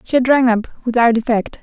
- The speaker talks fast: Yes, fast, 220 wpm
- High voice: Yes, high, 240 Hz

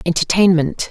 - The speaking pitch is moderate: Yes, medium, 175 Hz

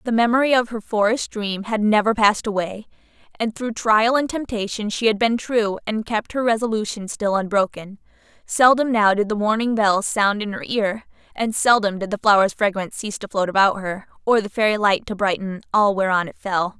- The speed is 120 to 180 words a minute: No, average, 200 wpm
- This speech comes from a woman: Yes, female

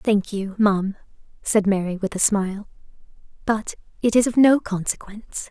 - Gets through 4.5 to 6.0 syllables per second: Yes, 5.0 syllables/s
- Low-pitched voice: No, high, 205 Hz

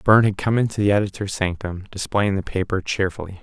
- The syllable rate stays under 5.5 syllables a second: No, 6.1 syllables/s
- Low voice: Yes, low, 100 Hz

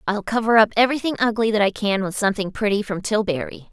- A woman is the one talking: Yes, female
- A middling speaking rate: No, fast, 210 wpm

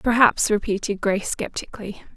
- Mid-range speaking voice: No, high, 210 Hz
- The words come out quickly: No, slow, 110 wpm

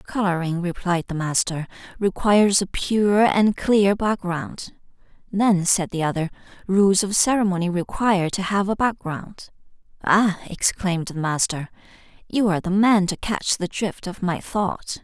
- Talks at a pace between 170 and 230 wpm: No, average, 150 wpm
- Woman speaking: Yes, female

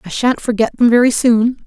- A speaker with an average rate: No, fast, 215 wpm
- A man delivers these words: No, female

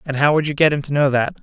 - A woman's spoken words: No, male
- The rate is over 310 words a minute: Yes, fast, 380 wpm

